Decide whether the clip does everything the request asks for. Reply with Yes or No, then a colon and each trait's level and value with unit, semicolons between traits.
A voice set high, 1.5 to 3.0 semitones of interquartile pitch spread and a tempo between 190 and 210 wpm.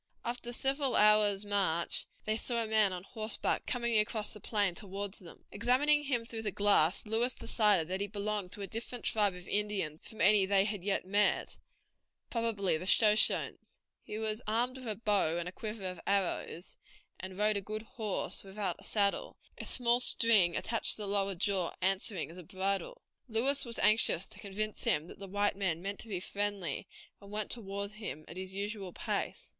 Yes: high, 205 Hz; narrow, 2.4 semitones; average, 195 wpm